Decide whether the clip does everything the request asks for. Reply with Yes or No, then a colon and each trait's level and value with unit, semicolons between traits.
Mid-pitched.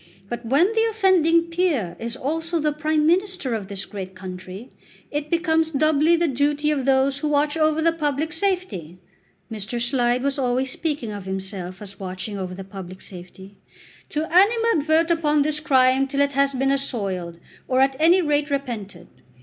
No: very high, 280 Hz